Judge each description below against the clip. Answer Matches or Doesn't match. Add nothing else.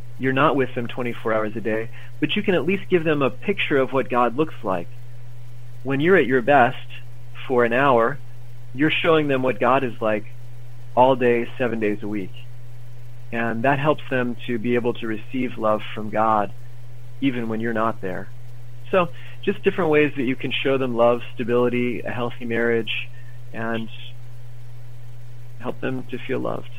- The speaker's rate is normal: Matches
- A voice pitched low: Matches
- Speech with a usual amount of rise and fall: Doesn't match